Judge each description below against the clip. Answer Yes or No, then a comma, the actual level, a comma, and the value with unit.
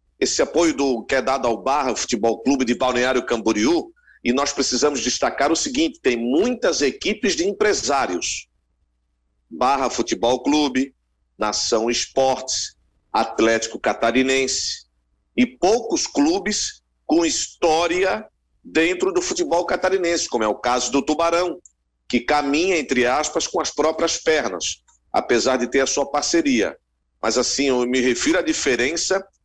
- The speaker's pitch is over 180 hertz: No, low, 135 Hz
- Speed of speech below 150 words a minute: Yes, average, 135 wpm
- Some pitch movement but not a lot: No, wide, 6.2 semitones